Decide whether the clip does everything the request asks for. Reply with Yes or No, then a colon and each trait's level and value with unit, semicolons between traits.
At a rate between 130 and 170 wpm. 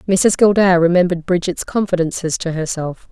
Yes: slow, 135 wpm